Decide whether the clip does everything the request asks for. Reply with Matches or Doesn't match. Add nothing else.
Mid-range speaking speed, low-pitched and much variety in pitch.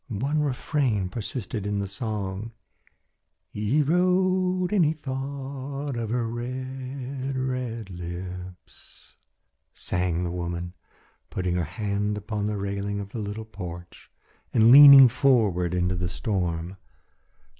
Doesn't match